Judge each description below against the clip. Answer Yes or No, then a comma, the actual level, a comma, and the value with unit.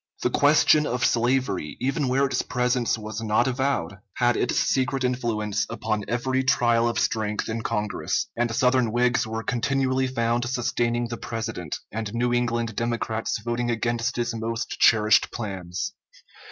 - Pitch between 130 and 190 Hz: No, low, 120 Hz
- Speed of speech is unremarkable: Yes, average, 150 wpm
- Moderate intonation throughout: No, narrow, 2.1 semitones